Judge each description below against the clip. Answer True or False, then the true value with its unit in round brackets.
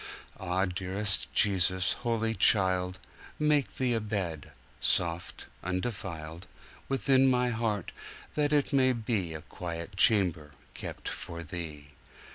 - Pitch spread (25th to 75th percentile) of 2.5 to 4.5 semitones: False (5.2 semitones)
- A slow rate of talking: True (100 wpm)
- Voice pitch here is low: True (95 Hz)